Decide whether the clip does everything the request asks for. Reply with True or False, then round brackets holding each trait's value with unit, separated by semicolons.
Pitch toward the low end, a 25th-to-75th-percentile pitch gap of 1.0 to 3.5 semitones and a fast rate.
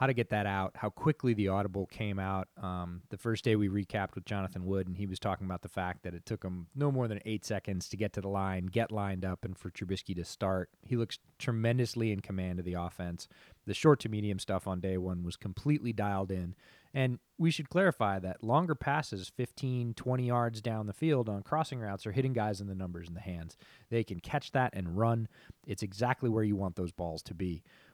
False (100 Hz; 4.0 semitones; 230 wpm)